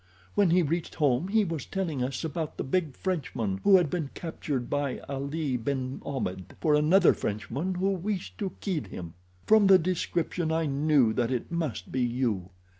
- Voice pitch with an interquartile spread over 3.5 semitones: Yes, wide, 5.6 semitones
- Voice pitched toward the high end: No, medium, 150 Hz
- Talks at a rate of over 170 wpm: Yes, average, 180 wpm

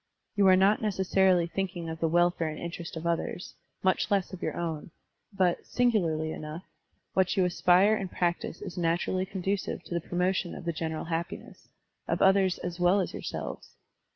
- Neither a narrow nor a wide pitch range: No, narrow, 2.1 semitones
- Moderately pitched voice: Yes, medium, 180 Hz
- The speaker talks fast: No, average, 185 wpm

